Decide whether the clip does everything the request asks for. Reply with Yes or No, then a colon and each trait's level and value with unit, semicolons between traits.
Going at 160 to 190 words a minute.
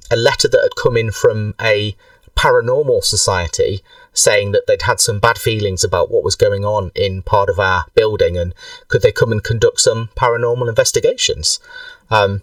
Yes: average, 180 wpm